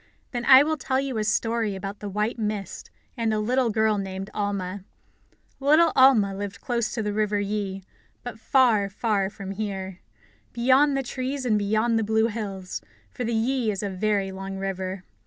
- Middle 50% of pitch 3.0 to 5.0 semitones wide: Yes, average, 3.4 semitones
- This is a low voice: No, high, 215 Hz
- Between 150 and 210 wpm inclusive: Yes, average, 180 wpm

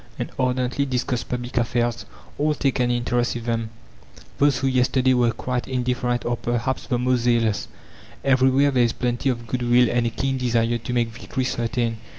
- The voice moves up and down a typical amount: No, narrow, 1.4 semitones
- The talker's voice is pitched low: Yes, low, 125 Hz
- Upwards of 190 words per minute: No, average, 180 wpm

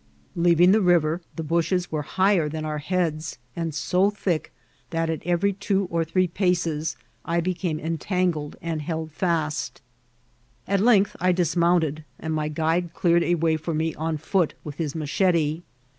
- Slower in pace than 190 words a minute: Yes, average, 165 wpm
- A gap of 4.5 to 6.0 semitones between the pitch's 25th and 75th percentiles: No, narrow, 2.4 semitones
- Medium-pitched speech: Yes, medium, 165 Hz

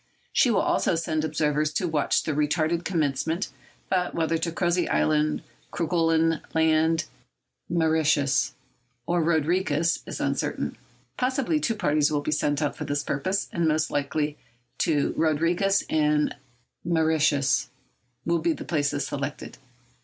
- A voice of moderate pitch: Yes, medium, 160 Hz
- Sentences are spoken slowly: Yes, slow, 130 wpm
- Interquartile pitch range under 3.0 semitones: Yes, narrow, 2.4 semitones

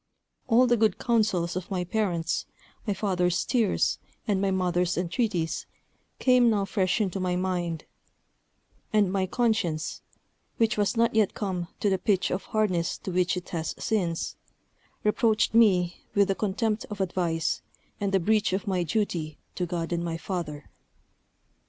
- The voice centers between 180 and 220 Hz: Yes, high, 190 Hz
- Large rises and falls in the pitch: No, average, 3.3 semitones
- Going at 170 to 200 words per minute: No, average, 155 wpm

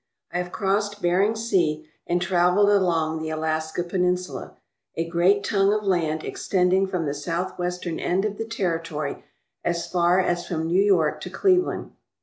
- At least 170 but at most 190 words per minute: No, average, 155 wpm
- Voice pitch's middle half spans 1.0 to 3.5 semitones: Yes, average, 2.8 semitones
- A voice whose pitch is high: No, medium, 180 Hz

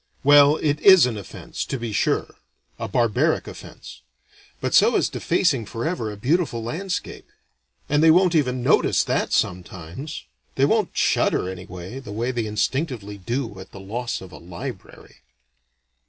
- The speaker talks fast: No, average, 155 wpm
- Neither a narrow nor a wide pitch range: No, wide, 6.3 semitones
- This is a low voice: Yes, low, 120 Hz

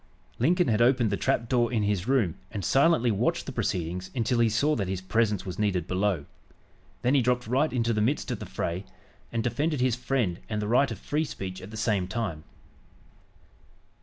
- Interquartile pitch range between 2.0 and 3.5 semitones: No, average, 4.5 semitones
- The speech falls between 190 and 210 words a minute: Yes, average, 200 wpm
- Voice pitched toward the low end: Yes, low, 115 Hz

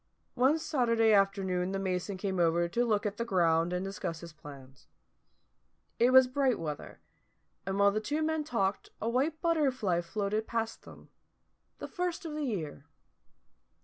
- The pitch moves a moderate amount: No, wide, 6.0 semitones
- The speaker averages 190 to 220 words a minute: No, average, 155 wpm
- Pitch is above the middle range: Yes, high, 205 Hz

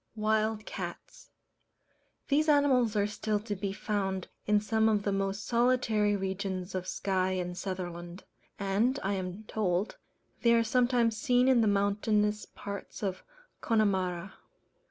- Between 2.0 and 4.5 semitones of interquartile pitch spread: Yes, narrow, 2.6 semitones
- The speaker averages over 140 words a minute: No, slow, 135 wpm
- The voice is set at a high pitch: Yes, high, 205 Hz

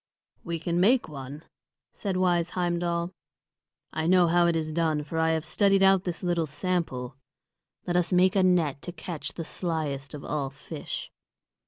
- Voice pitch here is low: No, medium, 170 Hz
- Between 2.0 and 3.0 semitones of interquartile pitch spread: Yes, narrow, 2.5 semitones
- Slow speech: No, average, 170 wpm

